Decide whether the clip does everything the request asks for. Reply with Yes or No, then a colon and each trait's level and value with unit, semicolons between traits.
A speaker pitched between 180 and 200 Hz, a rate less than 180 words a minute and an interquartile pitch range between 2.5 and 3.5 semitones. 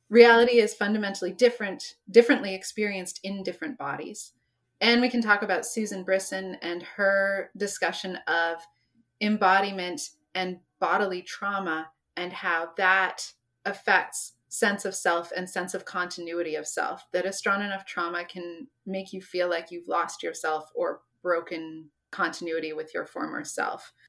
Yes: high, 190 Hz; average, 140 wpm; average, 2.8 semitones